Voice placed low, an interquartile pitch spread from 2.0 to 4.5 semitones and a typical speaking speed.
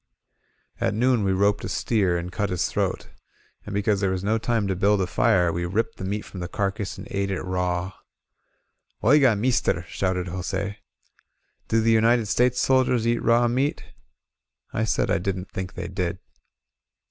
Yes: low, 100 Hz; average, 3.5 semitones; average, 175 wpm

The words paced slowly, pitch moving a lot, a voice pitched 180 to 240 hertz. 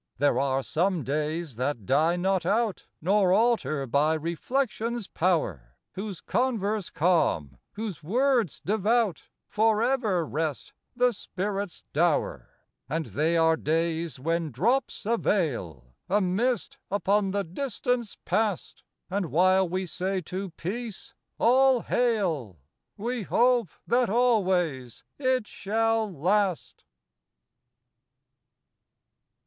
Yes: slow, 120 wpm; wide, 5.8 semitones; high, 190 Hz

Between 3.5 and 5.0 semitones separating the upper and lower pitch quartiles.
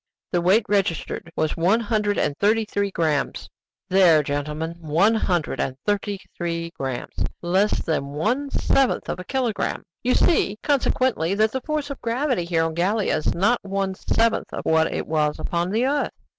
No: wide, 5.6 semitones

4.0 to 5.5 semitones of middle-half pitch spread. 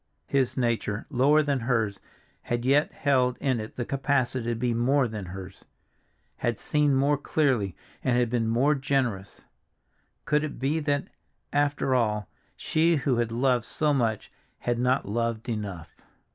No: average, 3.6 semitones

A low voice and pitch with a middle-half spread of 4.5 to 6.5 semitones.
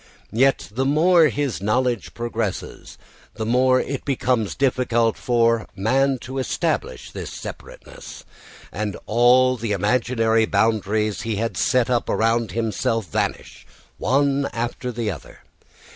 No: low, 115 Hz; average, 2.7 semitones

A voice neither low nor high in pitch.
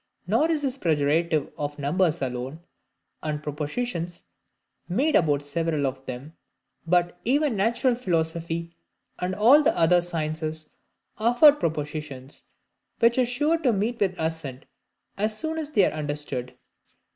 Yes: medium, 170 Hz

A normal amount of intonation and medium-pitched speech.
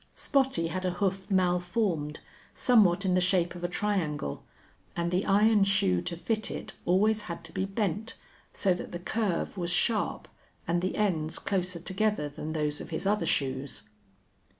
Yes: average, 3.2 semitones; medium, 180 Hz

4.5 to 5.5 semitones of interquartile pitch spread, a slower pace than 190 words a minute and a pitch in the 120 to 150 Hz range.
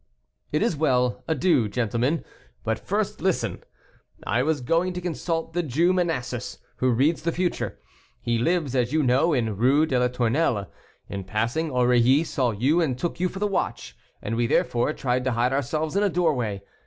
Yes: average, 5.2 semitones; average, 180 wpm; low, 135 Hz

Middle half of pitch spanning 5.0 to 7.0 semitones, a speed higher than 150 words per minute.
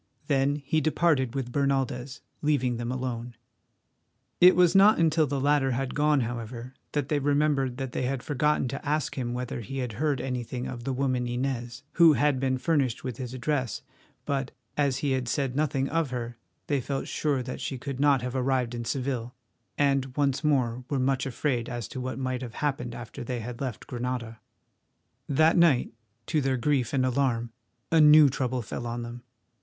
No: average, 2.7 semitones; average, 185 wpm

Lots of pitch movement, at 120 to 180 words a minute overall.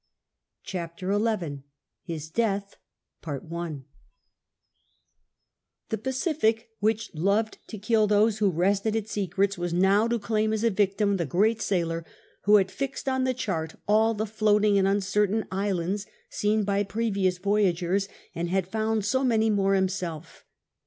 No: average, 2.9 semitones; average, 140 wpm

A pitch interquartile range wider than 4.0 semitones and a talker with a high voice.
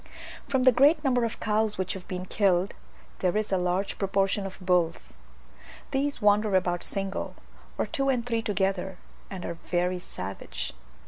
No: average, 3.6 semitones; high, 195 Hz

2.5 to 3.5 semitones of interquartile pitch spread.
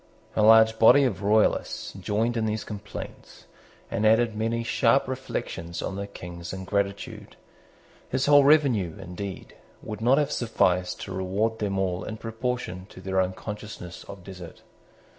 Yes: average, 3.2 semitones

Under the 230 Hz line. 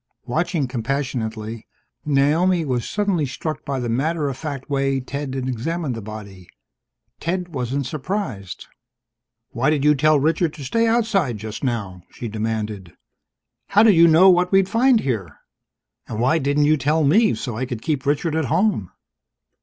Yes: medium, 140 Hz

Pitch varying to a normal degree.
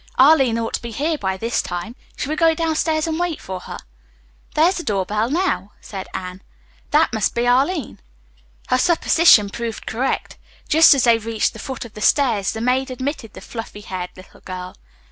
No: wide, 6.6 semitones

